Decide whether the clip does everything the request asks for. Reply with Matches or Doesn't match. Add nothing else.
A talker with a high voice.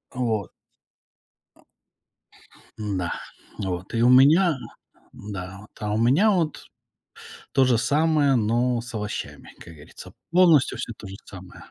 Doesn't match